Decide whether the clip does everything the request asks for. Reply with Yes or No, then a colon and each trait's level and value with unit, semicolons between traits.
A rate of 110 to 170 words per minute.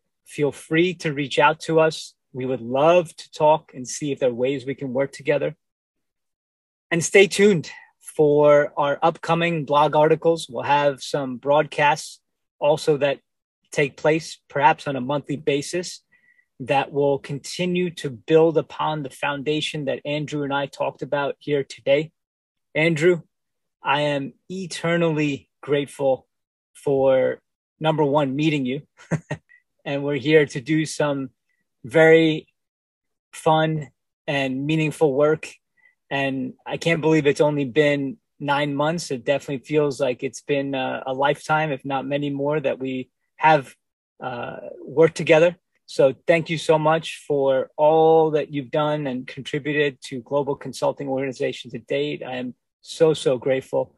Yes: average, 145 wpm